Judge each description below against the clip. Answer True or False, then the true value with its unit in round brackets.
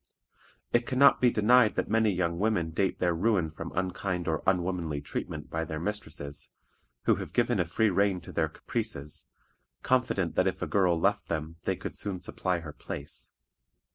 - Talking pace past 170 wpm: True (180 wpm)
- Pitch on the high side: False (90 Hz)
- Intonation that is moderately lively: True (4.1 semitones)